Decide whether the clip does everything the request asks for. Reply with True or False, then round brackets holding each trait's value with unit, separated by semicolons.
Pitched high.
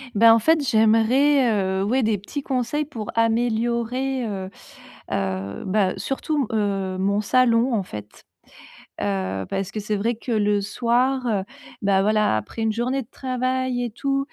True (225 Hz)